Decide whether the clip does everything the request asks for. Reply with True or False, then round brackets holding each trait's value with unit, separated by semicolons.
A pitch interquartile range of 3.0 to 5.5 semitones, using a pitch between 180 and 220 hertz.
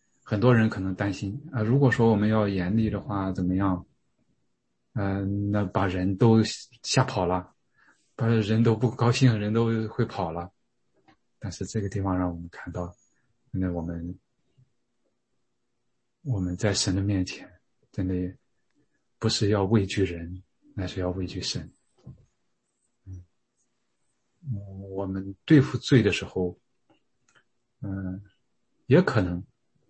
False (3.9 semitones; 100 Hz)